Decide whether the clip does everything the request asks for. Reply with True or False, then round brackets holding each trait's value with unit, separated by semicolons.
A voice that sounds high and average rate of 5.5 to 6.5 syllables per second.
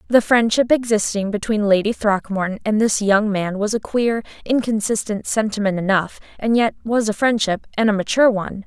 False (215 Hz; 5.3 syllables/s)